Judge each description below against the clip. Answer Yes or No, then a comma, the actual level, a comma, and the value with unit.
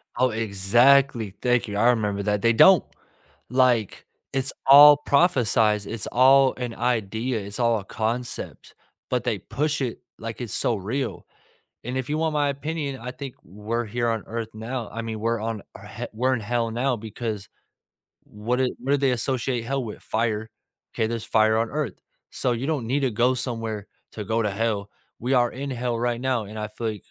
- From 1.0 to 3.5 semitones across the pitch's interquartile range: Yes, average, 2.9 semitones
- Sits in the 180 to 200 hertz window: No, low, 115 Hz